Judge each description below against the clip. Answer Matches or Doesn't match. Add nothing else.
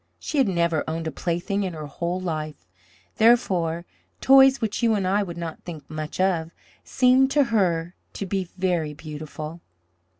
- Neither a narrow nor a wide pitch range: Matches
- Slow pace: Doesn't match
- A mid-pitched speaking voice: Matches